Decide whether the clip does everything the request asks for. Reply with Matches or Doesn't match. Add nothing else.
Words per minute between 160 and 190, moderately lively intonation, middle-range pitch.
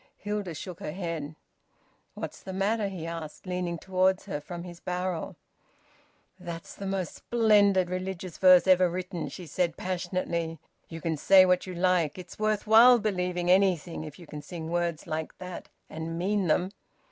Doesn't match